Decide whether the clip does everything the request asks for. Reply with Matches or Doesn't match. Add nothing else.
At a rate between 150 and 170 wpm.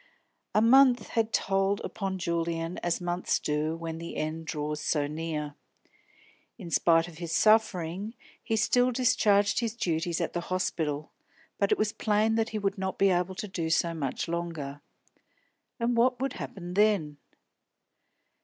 Matches